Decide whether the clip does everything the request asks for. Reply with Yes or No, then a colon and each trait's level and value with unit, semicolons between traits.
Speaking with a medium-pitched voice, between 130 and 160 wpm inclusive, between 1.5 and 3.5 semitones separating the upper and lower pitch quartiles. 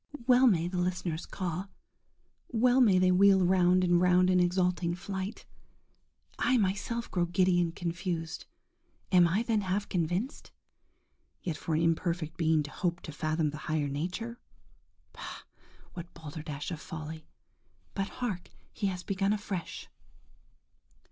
Yes: medium, 180 Hz; slow, 135 wpm; average, 2.7 semitones